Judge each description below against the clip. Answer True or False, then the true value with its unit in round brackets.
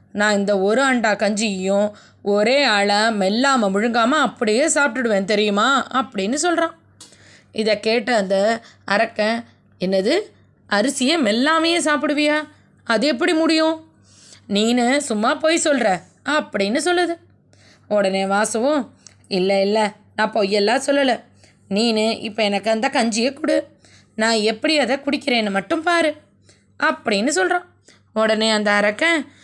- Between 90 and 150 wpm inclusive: True (110 wpm)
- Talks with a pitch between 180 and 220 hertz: False (230 Hz)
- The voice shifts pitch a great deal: True (6.0 semitones)